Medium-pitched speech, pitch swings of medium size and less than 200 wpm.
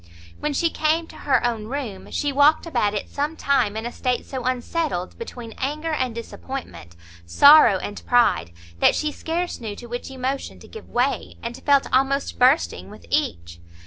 No: very high, 260 Hz; average, 4.4 semitones; average, 175 wpm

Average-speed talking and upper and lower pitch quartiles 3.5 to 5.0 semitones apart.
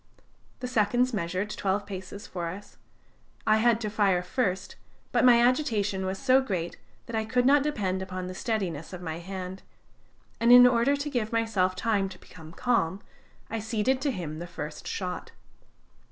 Yes: average, 170 wpm; average, 4.5 semitones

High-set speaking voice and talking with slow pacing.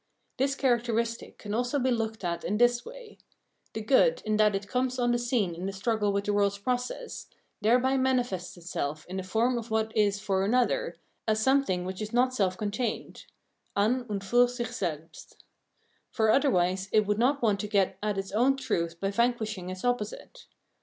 No: high, 220 Hz; average, 185 wpm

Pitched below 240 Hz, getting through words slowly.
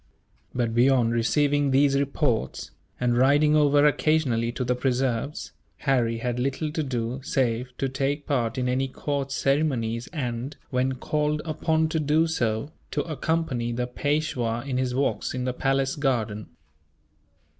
No: low, 135 Hz; average, 145 wpm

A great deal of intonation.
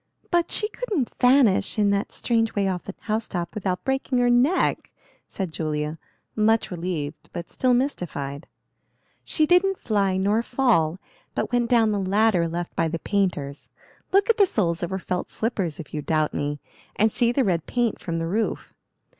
Yes: wide, 6.3 semitones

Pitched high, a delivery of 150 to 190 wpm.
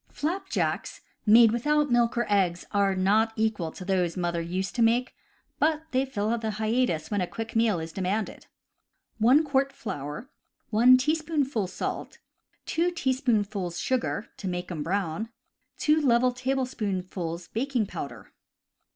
No: high, 220 Hz; average, 140 wpm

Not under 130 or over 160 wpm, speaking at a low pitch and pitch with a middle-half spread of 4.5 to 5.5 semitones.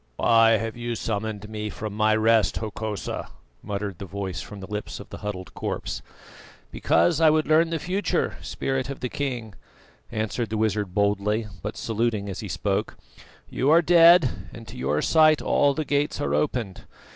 No: average, 175 wpm; low, 110 Hz; average, 4.8 semitones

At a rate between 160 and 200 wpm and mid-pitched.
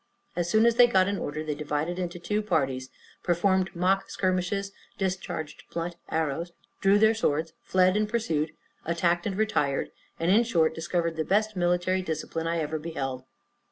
Yes: average, 165 wpm; medium, 175 Hz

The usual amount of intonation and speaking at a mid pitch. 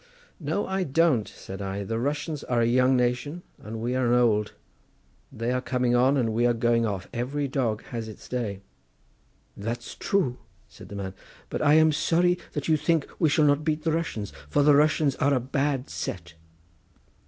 No: average, 4.4 semitones; low, 125 Hz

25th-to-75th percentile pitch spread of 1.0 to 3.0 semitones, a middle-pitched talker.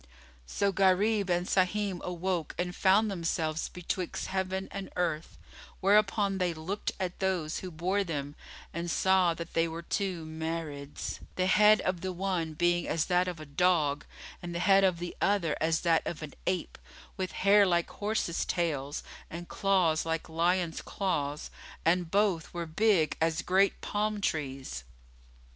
Yes: average, 2.7 semitones; medium, 175 Hz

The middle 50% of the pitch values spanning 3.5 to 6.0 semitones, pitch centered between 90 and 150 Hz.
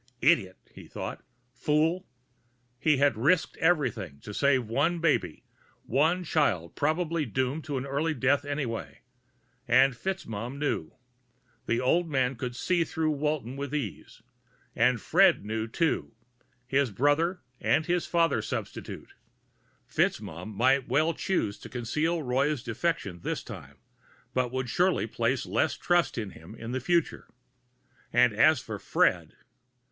Yes: average, 5.2 semitones; low, 135 Hz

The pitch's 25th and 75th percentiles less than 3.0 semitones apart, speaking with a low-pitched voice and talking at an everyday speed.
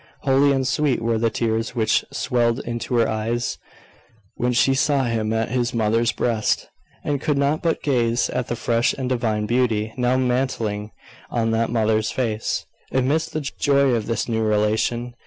Yes: narrow, 2.6 semitones; low, 120 Hz; average, 170 wpm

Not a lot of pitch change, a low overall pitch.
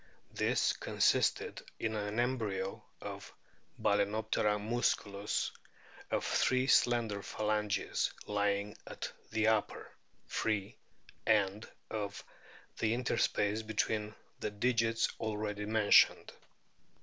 Yes: narrow, 1.4 semitones; low, 105 Hz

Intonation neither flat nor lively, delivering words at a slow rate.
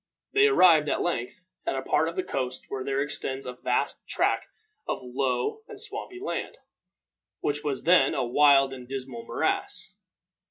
No: average, 4.7 semitones; average, 165 wpm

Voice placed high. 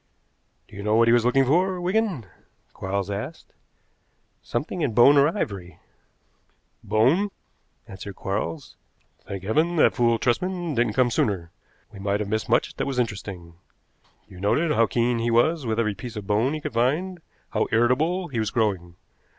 No: low, 115 Hz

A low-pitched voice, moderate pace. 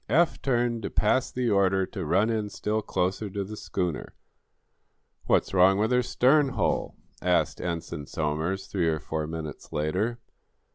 Yes: very low, 95 Hz; average, 155 wpm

